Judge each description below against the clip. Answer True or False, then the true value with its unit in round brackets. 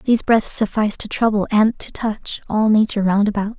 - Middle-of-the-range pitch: False (215 Hz)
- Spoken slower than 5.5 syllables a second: False (5.6 syllables/s)